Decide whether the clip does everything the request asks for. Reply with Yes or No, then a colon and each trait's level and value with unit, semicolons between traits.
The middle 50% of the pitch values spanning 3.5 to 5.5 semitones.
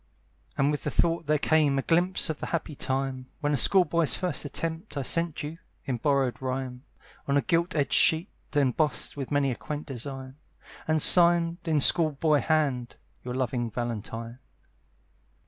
Yes: average, 3.8 semitones